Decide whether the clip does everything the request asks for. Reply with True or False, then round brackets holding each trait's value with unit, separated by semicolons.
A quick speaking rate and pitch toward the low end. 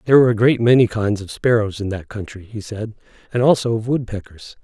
True (220 wpm; 110 Hz)